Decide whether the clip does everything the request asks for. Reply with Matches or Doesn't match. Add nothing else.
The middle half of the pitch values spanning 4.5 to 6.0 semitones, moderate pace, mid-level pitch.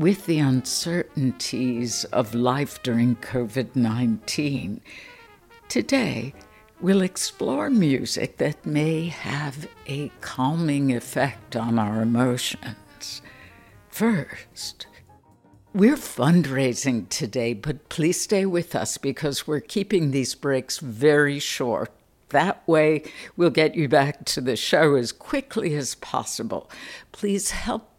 Doesn't match